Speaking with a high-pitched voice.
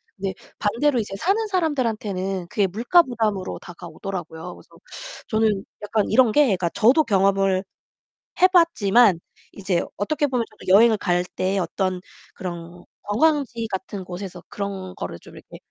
Yes: high, 200 Hz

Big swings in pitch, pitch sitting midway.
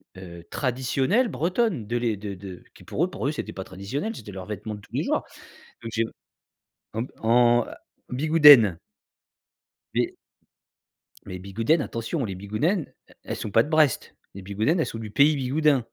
No: wide, 6.6 semitones; low, 120 Hz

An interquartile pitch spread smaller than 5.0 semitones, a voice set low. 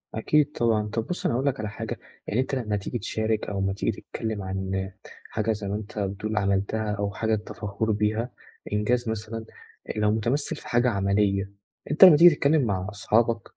Yes: narrow, 2.5 semitones; low, 110 Hz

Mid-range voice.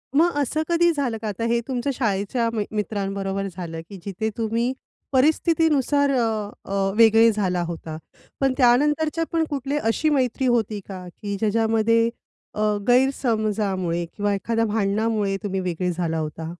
No: high, 225 Hz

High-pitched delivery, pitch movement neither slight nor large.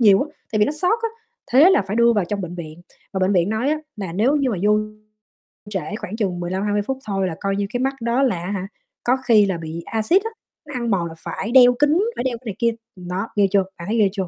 Yes: high, 210 Hz; average, 4.6 semitones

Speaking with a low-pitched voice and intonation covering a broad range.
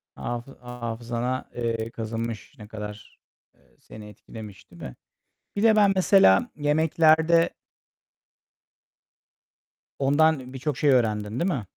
Yes: low, 120 Hz; wide, 6.0 semitones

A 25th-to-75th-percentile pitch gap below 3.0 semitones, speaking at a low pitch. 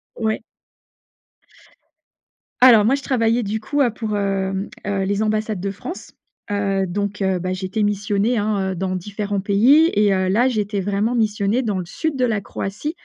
No: narrow, 2.4 semitones; high, 205 Hz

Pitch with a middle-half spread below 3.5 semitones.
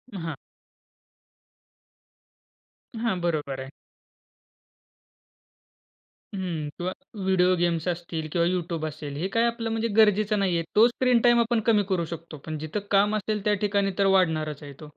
No: average, 4.7 semitones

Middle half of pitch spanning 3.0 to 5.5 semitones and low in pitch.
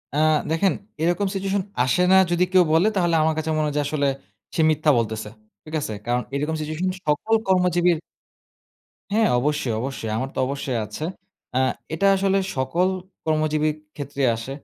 No: average, 4.5 semitones; medium, 155 Hz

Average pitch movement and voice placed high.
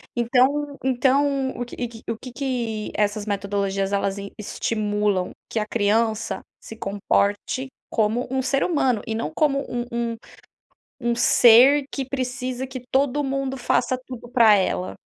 Yes: average, 3.9 semitones; high, 235 Hz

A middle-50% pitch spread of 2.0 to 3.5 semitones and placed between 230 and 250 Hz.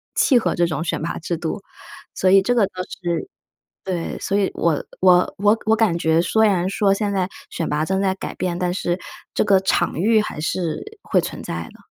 No: average, 3.0 semitones; high, 190 Hz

